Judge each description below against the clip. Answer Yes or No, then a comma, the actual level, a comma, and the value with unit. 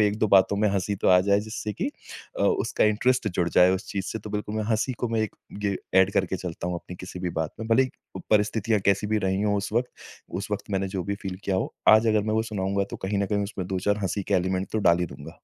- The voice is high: No, low, 100 Hz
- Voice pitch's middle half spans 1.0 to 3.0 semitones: Yes, narrow, 2.4 semitones